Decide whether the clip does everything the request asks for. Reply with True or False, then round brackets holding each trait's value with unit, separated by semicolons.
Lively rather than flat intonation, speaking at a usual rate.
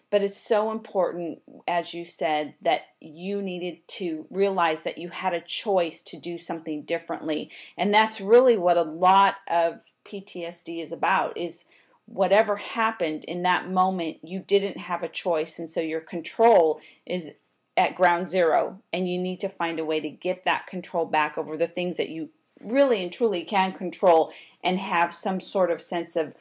False (2.6 semitones; 180 wpm)